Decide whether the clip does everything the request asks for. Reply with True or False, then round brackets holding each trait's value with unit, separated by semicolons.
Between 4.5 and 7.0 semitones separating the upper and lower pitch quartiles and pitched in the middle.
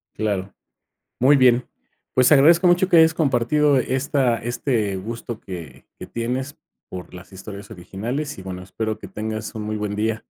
False (5.0 semitones; 115 Hz)